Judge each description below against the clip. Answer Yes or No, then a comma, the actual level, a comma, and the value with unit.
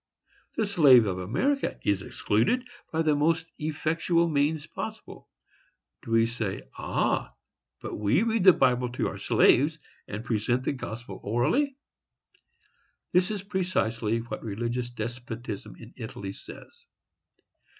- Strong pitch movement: Yes, wide, 6.7 semitones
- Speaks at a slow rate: Yes, slow, 125 wpm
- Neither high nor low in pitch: No, low, 125 Hz